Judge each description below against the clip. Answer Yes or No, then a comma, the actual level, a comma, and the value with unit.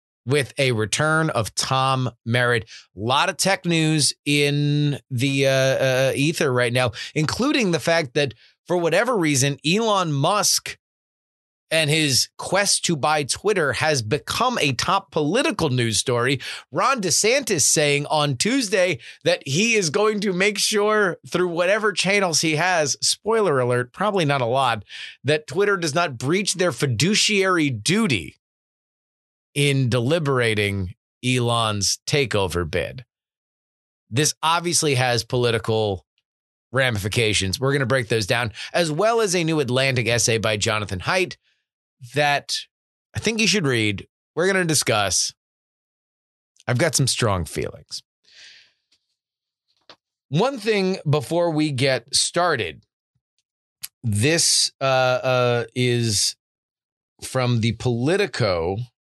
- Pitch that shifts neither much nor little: No, wide, 6.0 semitones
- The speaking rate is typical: No, slow, 125 wpm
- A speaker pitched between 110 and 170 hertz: Yes, medium, 140 Hz